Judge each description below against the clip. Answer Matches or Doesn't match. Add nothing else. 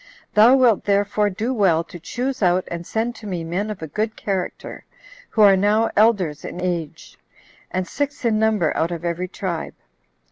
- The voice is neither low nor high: Doesn't match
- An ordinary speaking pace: Matches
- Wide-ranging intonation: Doesn't match